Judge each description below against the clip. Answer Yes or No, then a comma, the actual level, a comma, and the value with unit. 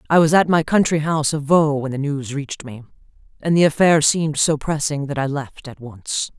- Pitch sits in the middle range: Yes, medium, 145 Hz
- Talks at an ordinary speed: No, fast, 225 wpm